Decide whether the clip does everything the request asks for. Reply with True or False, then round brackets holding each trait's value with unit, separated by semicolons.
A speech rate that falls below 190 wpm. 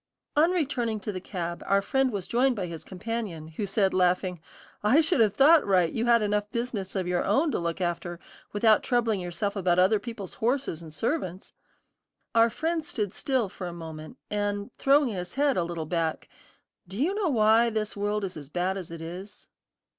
False (195 wpm)